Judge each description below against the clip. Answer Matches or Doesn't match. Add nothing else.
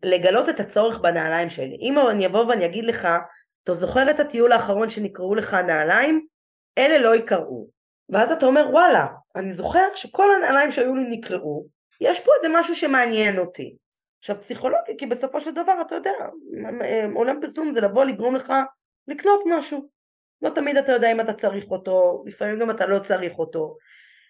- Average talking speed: Doesn't match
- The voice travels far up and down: Matches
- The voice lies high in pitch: Matches